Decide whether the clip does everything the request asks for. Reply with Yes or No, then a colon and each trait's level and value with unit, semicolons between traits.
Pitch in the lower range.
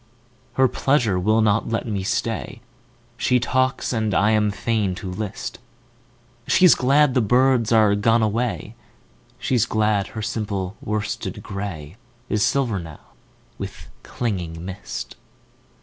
Yes: low, 115 Hz